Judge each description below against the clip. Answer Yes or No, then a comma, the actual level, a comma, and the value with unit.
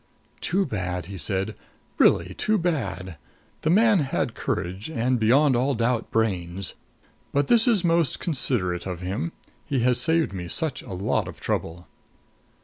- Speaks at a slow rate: No, average, 150 wpm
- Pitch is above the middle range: No, low, 120 Hz